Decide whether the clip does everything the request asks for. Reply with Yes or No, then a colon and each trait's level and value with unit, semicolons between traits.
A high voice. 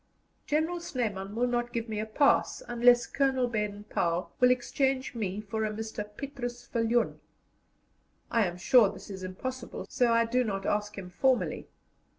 Yes: high, 230 Hz